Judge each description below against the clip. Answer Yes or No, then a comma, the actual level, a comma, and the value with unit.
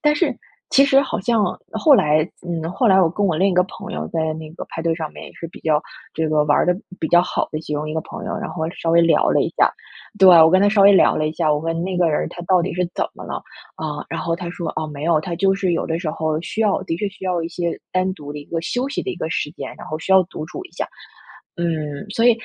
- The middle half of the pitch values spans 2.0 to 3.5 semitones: Yes, average, 3.2 semitones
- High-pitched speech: No, medium, 170 Hz